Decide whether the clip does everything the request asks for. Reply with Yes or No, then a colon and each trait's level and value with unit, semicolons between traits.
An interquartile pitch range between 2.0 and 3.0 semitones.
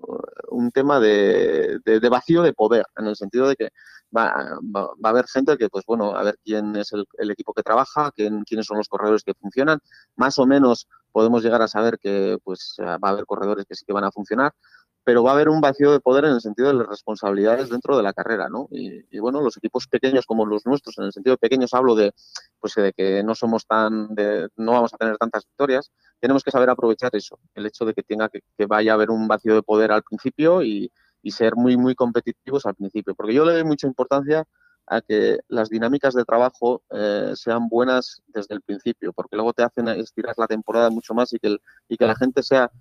No: average, 3.5 semitones